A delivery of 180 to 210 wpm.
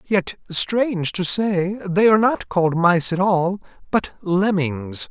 No: average, 155 wpm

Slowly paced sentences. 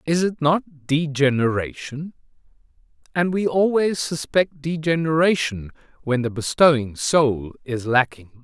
Yes: slow, 100 wpm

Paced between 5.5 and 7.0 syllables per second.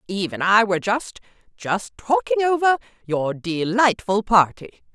No: 4.6 syllables/s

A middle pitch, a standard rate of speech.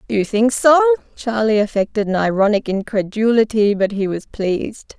No: high, 220 Hz; average, 145 wpm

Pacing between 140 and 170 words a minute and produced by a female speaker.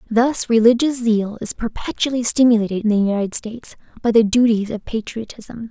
Yes: average, 160 wpm; female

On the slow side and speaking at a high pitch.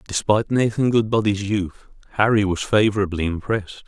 No: slow, 125 wpm; low, 105 Hz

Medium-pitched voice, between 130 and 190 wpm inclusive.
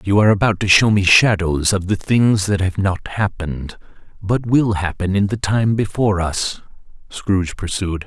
No: low, 100 Hz; average, 180 wpm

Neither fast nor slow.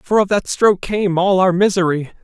No: fast, 215 wpm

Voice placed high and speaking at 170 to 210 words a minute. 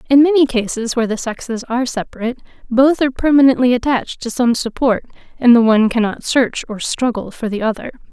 Yes: high, 240 Hz; average, 185 wpm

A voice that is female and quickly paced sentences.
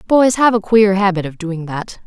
Yes: female; fast, 230 wpm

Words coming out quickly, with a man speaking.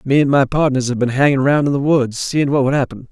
Yes: fast, 290 wpm; male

